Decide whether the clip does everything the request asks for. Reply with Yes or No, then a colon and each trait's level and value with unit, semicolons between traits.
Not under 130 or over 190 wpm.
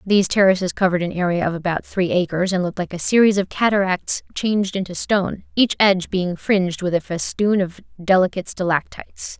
Yes: average, 185 wpm